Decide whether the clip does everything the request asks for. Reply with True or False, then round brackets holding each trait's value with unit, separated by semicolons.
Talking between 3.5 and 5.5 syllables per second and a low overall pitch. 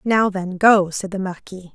False (4.5 syllables/s; 190 Hz)